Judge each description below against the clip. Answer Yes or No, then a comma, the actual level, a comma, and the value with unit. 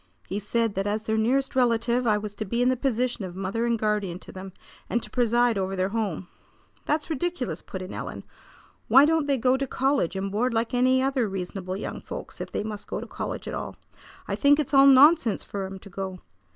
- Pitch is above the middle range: Yes, high, 225 Hz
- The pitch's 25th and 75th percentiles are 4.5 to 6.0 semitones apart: Yes, average, 4.8 semitones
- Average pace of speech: No, fast, 225 wpm